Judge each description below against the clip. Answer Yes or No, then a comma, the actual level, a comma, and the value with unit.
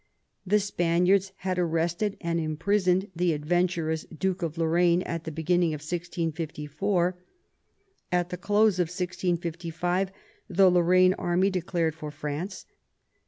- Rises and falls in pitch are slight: Yes, narrow, 2.0 semitones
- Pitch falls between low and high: Yes, medium, 175 Hz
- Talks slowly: Yes, slow, 120 wpm